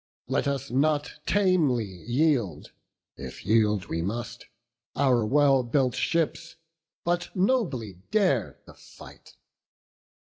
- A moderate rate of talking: No, slow, 105 wpm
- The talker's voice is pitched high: No, low, 135 Hz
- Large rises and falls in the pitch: Yes, wide, 6.3 semitones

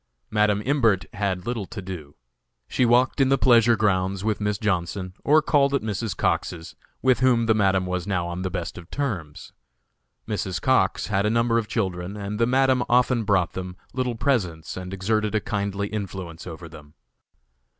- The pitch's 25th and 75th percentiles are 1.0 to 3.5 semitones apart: No, average, 4.2 semitones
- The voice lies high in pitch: No, low, 105 Hz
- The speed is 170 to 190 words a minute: Yes, average, 180 wpm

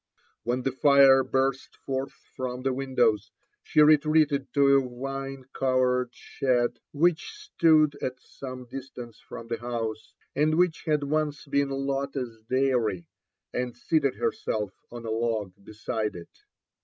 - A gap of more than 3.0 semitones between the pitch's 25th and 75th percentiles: No, narrow, 2.6 semitones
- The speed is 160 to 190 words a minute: No, slow, 135 wpm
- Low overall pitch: Yes, low, 130 Hz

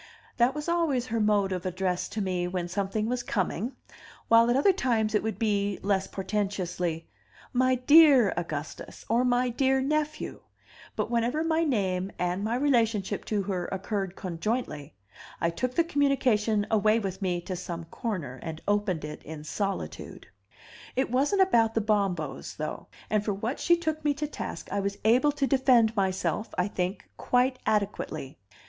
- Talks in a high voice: Yes, high, 210 Hz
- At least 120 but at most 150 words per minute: No, average, 165 wpm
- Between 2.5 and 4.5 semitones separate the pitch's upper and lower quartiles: No, average, 5.3 semitones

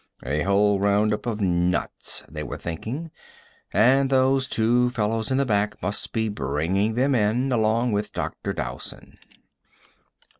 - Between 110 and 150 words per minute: Yes, average, 140 wpm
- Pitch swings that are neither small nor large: Yes, average, 4.0 semitones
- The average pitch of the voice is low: Yes, low, 110 Hz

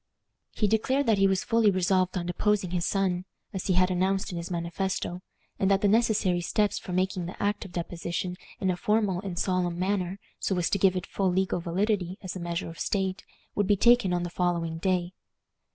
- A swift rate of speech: Yes, fast, 210 wpm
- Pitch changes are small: Yes, narrow, 2.1 semitones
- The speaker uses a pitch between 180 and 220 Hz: Yes, medium, 185 Hz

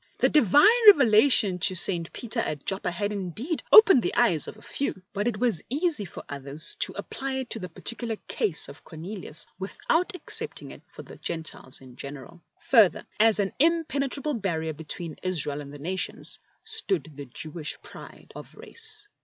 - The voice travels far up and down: Yes, wide, 8.7 semitones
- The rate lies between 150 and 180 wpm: Yes, average, 170 wpm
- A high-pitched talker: Yes, high, 200 Hz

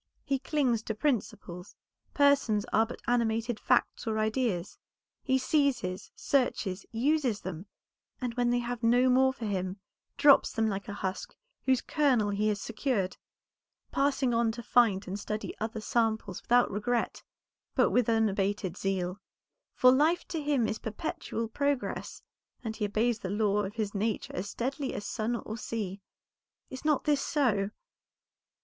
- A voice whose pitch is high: Yes, high, 225 Hz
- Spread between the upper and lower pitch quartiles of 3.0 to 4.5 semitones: Yes, average, 3.8 semitones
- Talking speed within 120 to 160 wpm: Yes, average, 155 wpm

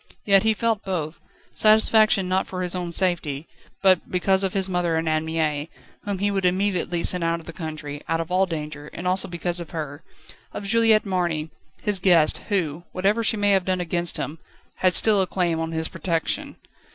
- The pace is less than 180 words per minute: No, average, 200 wpm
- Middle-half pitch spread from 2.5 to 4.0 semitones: Yes, average, 3.0 semitones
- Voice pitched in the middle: Yes, medium, 180 Hz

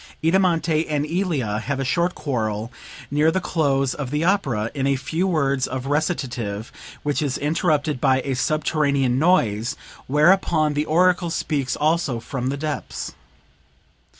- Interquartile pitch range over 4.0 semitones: No, average, 3.7 semitones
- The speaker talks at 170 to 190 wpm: No, average, 145 wpm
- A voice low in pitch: No, medium, 145 Hz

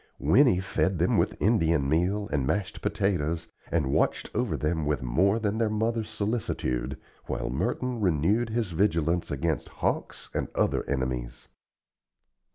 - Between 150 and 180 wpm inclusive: No, average, 140 wpm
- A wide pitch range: Yes, wide, 6.4 semitones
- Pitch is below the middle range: Yes, very low, 90 Hz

